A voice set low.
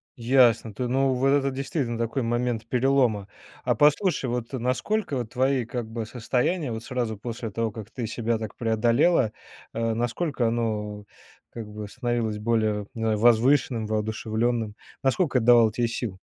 Yes: low, 120 Hz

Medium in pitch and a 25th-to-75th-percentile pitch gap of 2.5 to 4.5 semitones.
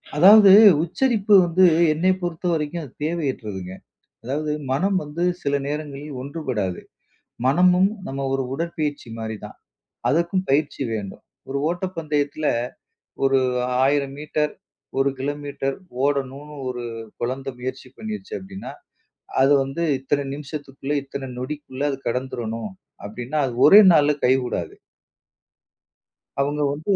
Yes: medium, 145 Hz; average, 3.8 semitones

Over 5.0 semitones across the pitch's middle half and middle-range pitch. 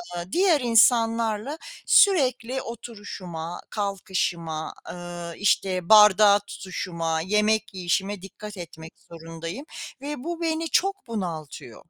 No: wide, 5.4 semitones; high, 205 Hz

